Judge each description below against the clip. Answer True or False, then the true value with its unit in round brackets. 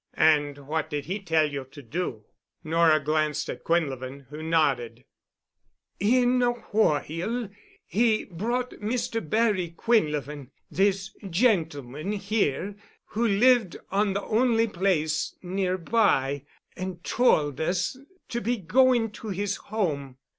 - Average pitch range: False (6.3 semitones)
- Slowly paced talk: True (115 wpm)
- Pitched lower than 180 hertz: False (185 Hz)